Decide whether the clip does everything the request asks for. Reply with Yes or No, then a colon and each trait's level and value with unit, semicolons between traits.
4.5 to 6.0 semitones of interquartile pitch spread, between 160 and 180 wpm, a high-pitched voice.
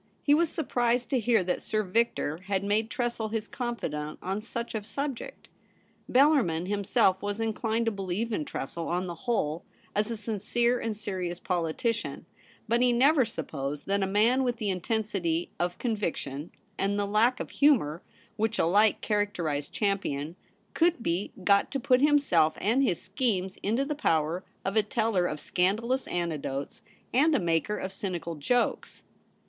Yes: average, 5.0 semitones; average, 165 wpm; high, 205 Hz